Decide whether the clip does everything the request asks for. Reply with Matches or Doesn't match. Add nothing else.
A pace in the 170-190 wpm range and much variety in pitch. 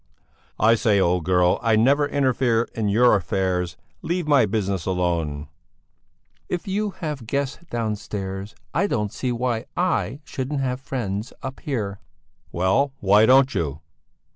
Doesn't match